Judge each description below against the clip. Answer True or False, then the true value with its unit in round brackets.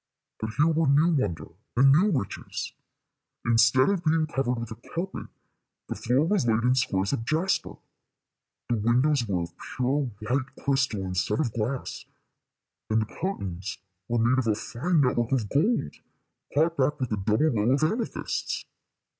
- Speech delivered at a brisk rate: False (165 wpm)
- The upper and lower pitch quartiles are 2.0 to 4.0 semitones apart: False (5.5 semitones)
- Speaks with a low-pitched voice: True (130 Hz)